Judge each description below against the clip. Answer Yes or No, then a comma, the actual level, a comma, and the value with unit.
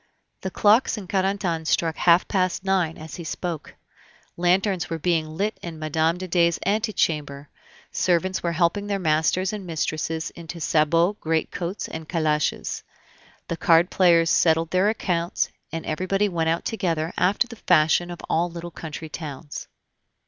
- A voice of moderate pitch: Yes, medium, 170 Hz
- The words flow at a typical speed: Yes, average, 150 wpm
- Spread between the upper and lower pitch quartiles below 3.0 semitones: Yes, narrow, 2.5 semitones